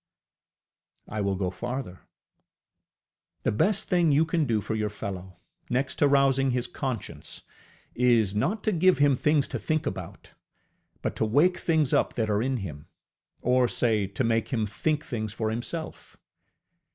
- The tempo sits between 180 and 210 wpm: No, average, 160 wpm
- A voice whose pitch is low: Yes, low, 125 Hz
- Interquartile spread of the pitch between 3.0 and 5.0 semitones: No, wide, 5.6 semitones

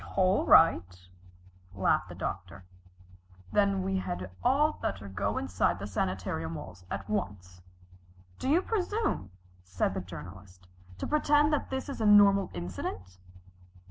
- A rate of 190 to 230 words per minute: No, slow, 135 wpm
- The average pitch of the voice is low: Yes, low, 100 Hz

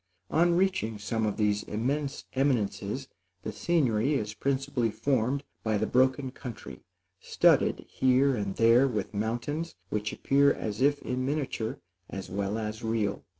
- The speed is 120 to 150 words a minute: Yes, average, 145 wpm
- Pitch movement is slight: No, average, 4.4 semitones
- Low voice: Yes, low, 120 Hz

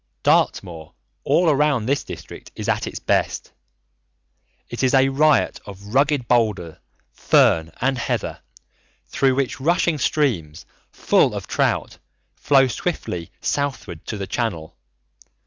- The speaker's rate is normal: No, slow, 125 wpm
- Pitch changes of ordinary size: No, wide, 6.1 semitones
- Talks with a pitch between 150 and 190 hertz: No, low, 125 Hz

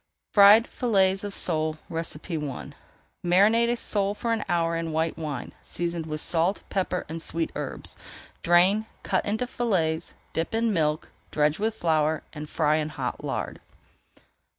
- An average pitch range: Yes, average, 4.4 semitones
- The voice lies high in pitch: No, medium, 170 Hz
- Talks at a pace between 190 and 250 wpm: No, average, 150 wpm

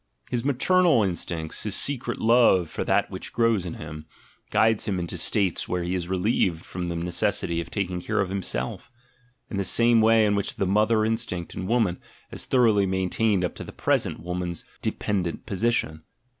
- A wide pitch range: No, average, 4.2 semitones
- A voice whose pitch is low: Yes, very low, 95 Hz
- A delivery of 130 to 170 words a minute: No, average, 180 wpm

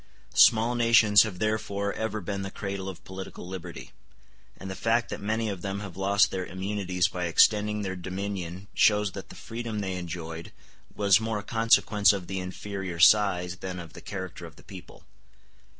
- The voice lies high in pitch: No, low, 100 Hz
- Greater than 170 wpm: Yes, average, 180 wpm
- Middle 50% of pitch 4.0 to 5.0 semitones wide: No, narrow, 2.4 semitones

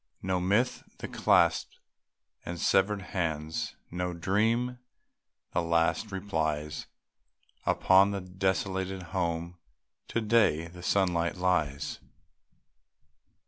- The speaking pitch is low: Yes, very low, 90 Hz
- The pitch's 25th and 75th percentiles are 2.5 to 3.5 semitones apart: Yes, average, 2.8 semitones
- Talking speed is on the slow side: Yes, slow, 95 wpm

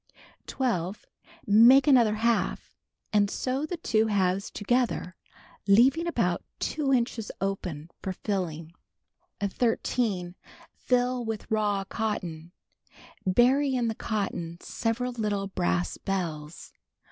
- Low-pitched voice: No, high, 215 Hz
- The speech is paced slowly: Yes, slow, 105 wpm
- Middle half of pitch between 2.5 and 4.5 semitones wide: No, average, 4.9 semitones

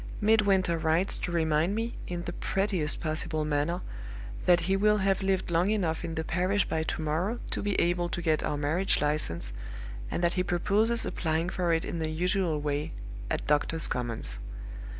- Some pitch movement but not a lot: Yes, average, 3.4 semitones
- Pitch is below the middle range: No, medium, 170 Hz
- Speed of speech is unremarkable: Yes, average, 180 wpm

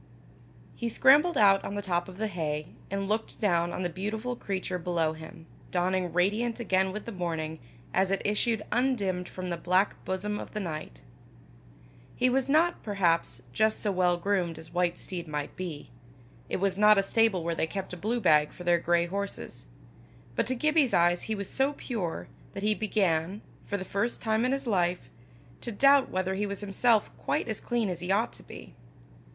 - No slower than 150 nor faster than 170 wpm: No, average, 195 wpm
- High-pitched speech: Yes, high, 195 Hz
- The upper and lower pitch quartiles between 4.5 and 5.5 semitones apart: No, average, 3.8 semitones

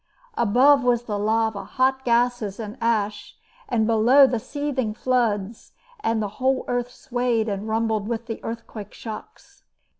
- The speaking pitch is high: Yes, high, 230 Hz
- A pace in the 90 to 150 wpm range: Yes, average, 145 wpm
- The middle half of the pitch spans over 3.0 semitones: No, narrow, 2.4 semitones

